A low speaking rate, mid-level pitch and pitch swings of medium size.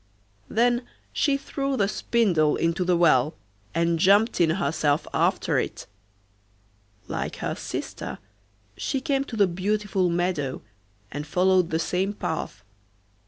Yes: slow, 125 wpm; medium, 180 Hz; average, 4.6 semitones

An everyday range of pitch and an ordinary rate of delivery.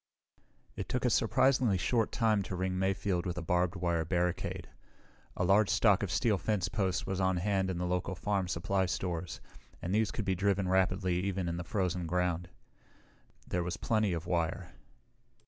No: narrow, 1.9 semitones; average, 180 wpm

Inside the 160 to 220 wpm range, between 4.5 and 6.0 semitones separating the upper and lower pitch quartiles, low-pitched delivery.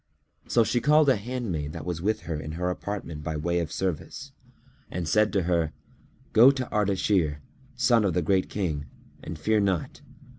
Yes: average, 180 wpm; average, 5.1 semitones; very low, 90 Hz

